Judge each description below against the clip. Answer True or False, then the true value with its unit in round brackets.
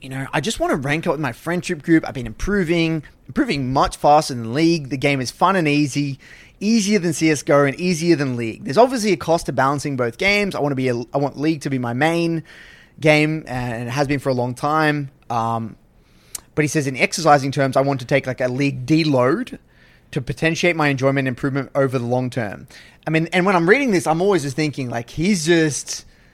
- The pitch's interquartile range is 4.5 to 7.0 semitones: False (4.0 semitones)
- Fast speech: True (230 wpm)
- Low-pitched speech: False (145 Hz)